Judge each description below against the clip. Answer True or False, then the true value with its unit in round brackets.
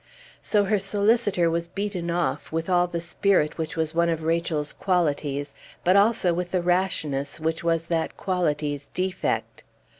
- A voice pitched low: False (170 Hz)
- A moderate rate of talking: True (155 wpm)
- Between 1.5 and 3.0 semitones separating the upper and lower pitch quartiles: True (2.6 semitones)